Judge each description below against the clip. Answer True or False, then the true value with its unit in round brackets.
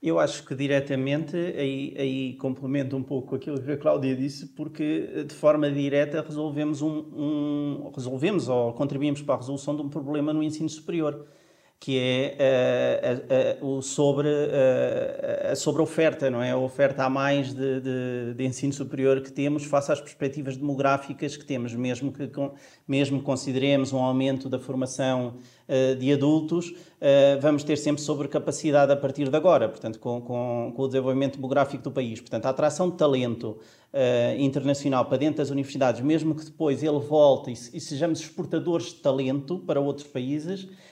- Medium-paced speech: True (175 wpm)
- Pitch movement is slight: True (2.3 semitones)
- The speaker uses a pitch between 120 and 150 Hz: True (140 Hz)